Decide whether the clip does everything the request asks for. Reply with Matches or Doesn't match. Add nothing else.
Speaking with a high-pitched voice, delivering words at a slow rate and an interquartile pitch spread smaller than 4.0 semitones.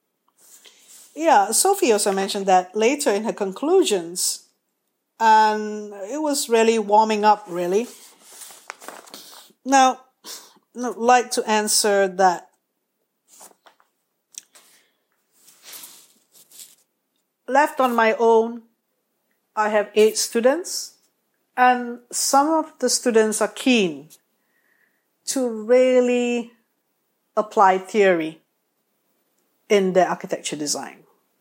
Matches